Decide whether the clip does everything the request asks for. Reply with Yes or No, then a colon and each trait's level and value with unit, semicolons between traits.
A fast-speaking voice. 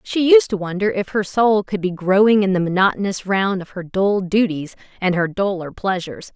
Yes: fast, 210 wpm